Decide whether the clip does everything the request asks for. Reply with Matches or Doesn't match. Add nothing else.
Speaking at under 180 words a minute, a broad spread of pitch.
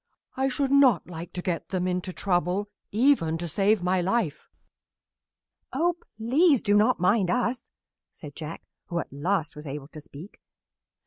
Matches